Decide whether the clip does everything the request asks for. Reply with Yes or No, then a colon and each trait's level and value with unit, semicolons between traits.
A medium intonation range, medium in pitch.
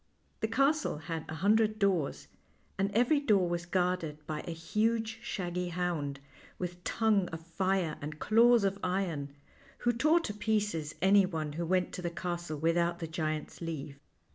Yes: average, 4.5 semitones; medium, 180 Hz